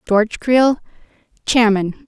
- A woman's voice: Yes, female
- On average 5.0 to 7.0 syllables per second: No, 4.1 syllables/s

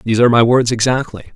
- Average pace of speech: No, fast, 220 wpm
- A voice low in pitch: Yes, low, 120 Hz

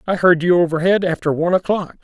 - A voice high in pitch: No, medium, 175 Hz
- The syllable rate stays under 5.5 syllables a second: No, 6.5 syllables/s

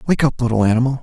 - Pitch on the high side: No, low, 125 Hz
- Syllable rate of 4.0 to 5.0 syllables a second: No, 8.1 syllables/s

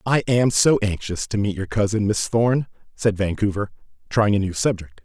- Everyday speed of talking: Yes, average, 190 wpm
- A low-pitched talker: Yes, low, 105 Hz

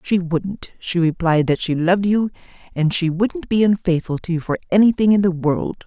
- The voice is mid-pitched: Yes, medium, 180 Hz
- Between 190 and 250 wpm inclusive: Yes, fast, 205 wpm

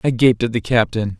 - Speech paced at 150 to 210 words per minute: No, fast, 250 wpm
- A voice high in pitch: No, low, 115 Hz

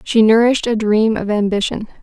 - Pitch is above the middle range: Yes, high, 220 Hz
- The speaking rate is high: No, average, 180 wpm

